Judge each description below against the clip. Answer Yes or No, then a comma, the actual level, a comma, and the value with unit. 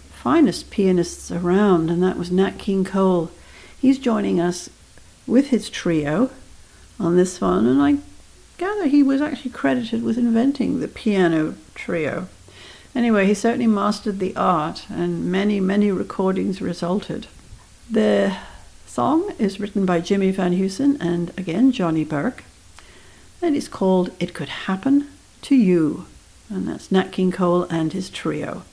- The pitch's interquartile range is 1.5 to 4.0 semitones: No, average, 5.1 semitones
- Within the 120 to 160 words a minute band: Yes, average, 145 wpm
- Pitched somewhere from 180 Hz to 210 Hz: Yes, high, 190 Hz